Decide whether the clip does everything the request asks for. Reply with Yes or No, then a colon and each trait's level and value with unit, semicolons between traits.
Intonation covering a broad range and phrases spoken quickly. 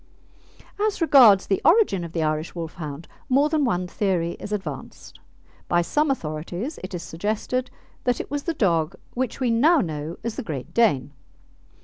No: wide, 7.7 semitones; average, 165 wpm